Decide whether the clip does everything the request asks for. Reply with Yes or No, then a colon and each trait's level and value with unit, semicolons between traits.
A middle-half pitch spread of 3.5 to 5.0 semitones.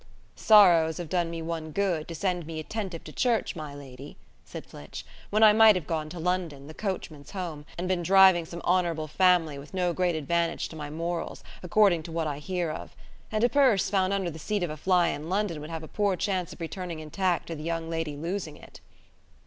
No: average, 3.0 semitones